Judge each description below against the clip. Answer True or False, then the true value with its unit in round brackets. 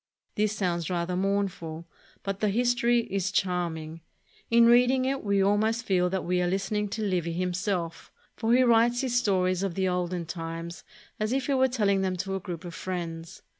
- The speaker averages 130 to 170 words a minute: False (190 wpm)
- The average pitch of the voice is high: True (195 Hz)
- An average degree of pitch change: True (4.0 semitones)